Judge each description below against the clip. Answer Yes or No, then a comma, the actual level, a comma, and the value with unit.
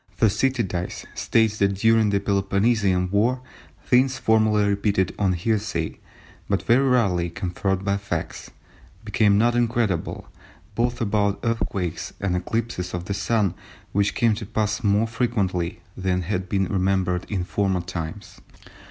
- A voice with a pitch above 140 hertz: No, low, 100 Hz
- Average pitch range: Yes, average, 3.2 semitones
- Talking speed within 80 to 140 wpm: Yes, slow, 135 wpm